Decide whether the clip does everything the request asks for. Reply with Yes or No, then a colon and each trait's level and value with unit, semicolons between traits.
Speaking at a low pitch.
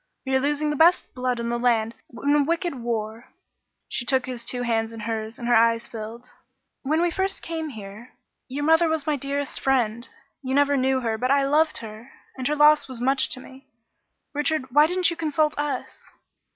No: very high, 265 Hz